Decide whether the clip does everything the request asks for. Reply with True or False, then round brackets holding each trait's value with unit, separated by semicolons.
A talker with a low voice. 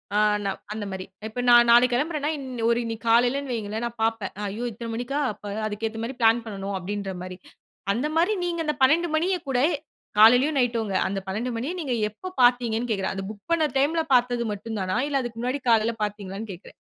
False (235 Hz)